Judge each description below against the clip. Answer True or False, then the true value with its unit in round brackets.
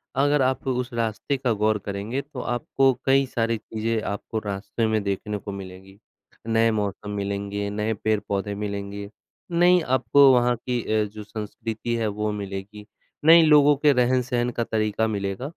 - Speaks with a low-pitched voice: True (110 Hz)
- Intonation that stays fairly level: False (3.7 semitones)